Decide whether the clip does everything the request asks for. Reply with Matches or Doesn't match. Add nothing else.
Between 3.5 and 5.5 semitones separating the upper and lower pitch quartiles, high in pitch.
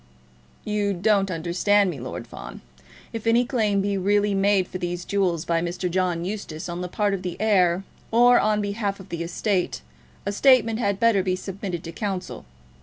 Doesn't match